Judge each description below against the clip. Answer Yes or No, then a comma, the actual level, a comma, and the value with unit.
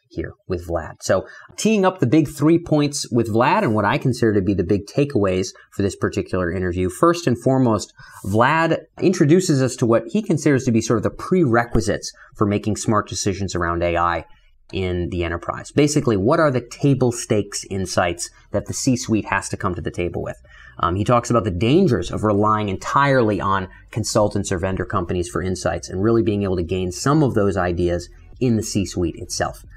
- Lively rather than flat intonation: Yes, wide, 5.7 semitones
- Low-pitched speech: Yes, low, 110 Hz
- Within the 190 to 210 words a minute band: Yes, average, 200 wpm